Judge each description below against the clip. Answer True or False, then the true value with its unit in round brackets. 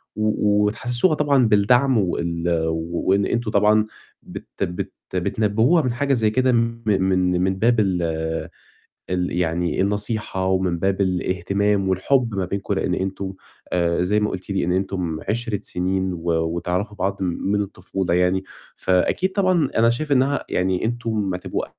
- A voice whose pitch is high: False (100 Hz)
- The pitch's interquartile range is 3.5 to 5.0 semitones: True (3.9 semitones)